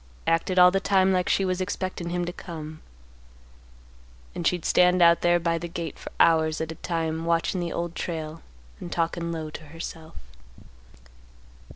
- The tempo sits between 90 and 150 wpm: No, average, 170 wpm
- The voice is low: No, medium, 170 Hz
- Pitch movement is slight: Yes, narrow, 1.6 semitones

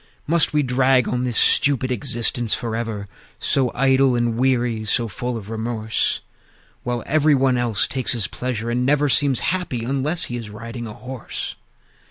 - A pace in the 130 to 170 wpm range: Yes, average, 165 wpm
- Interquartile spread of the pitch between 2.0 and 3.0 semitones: Yes, narrow, 2.4 semitones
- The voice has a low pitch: Yes, low, 125 Hz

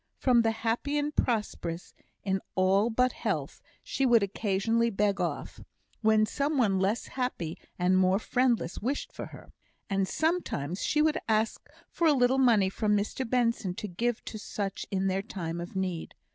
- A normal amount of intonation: Yes, average, 4.6 semitones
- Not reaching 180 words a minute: Yes, average, 170 wpm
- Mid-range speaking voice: No, high, 215 Hz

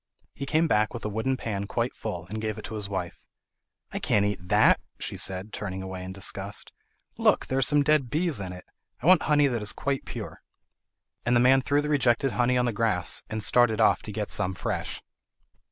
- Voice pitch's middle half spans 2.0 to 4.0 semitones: No, average, 4.8 semitones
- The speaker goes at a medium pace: No, fast, 220 wpm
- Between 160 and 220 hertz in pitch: No, low, 110 Hz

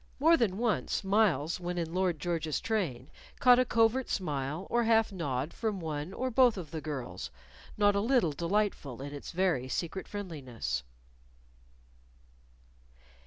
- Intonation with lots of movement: Yes, wide, 6.8 semitones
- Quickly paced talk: No, average, 145 wpm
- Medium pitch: Yes, medium, 180 Hz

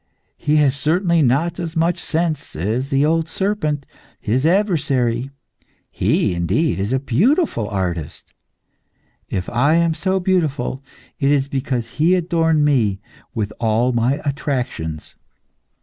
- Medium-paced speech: No, slow, 130 wpm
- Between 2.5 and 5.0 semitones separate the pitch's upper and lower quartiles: No, wide, 5.6 semitones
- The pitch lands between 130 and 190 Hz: Yes, medium, 140 Hz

